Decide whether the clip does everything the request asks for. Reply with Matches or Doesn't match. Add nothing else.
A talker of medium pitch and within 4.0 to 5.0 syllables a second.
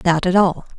Doesn't match